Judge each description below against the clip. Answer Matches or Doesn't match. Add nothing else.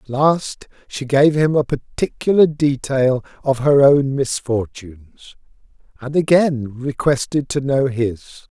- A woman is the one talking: Doesn't match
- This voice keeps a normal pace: Doesn't match